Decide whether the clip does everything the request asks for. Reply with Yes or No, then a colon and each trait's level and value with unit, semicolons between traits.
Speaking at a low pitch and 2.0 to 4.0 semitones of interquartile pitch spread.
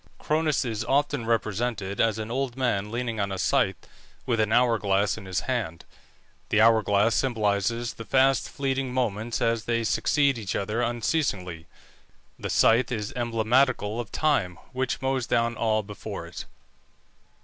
Yes: low, 115 Hz; average, 3.2 semitones